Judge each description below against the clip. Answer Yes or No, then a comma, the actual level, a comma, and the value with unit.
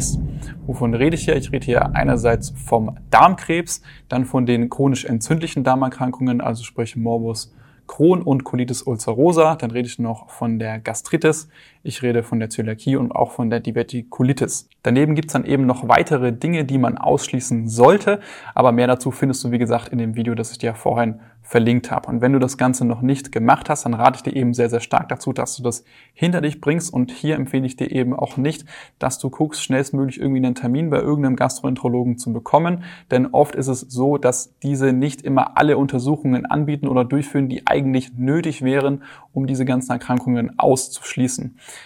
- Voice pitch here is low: Yes, low, 130 Hz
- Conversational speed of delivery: No, fast, 195 wpm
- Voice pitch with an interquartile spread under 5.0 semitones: Yes, average, 2.7 semitones